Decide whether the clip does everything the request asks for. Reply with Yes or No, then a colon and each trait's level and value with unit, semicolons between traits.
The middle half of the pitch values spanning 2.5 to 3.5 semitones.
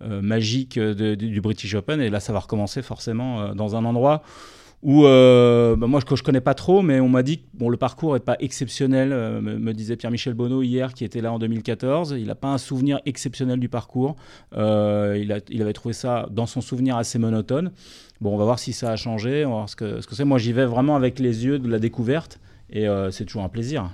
Yes: average, 3.2 semitones